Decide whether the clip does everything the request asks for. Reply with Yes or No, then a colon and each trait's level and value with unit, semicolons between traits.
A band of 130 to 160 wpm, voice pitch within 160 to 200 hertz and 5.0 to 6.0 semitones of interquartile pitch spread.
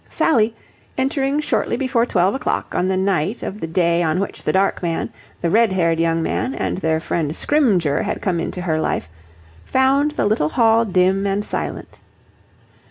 No: average, 175 wpm; high, 190 Hz; wide, 5.6 semitones